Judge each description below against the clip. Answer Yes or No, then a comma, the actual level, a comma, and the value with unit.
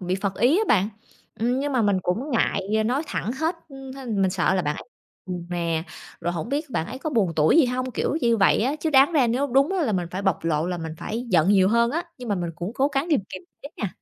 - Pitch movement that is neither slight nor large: No, wide, 6.6 semitones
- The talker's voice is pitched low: No, high, 225 Hz